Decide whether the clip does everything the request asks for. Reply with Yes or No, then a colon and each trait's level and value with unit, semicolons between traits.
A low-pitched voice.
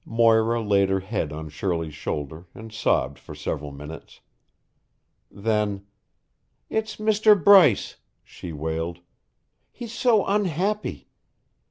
Yes: low, 105 Hz